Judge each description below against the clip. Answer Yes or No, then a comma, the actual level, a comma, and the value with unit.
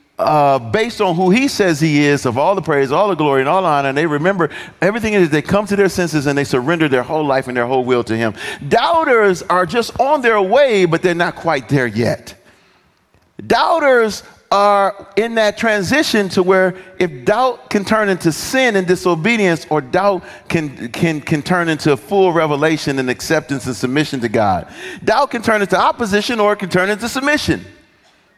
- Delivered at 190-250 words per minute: Yes, average, 200 wpm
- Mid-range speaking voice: Yes, medium, 180 Hz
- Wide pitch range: Yes, wide, 5.7 semitones